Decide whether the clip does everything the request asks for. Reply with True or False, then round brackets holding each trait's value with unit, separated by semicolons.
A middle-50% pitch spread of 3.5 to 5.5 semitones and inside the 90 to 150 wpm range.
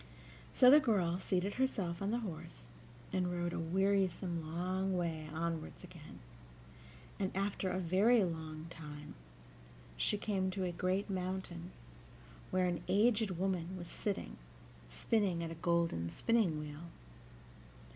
False (2.7 semitones; 135 wpm)